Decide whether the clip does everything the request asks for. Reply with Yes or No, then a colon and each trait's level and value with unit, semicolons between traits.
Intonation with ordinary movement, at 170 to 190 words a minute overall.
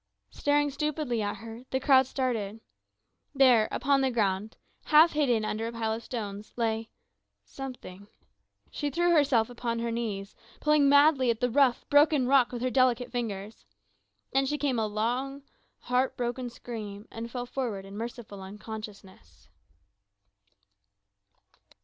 No: average, 3.6 semitones; average, 140 wpm